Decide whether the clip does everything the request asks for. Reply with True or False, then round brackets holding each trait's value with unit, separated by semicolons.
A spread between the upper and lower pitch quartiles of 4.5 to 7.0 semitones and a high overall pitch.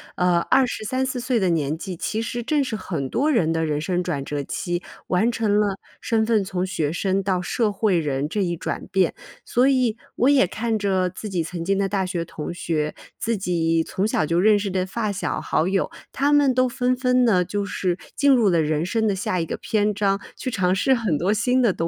True (4.8 semitones; 195 Hz)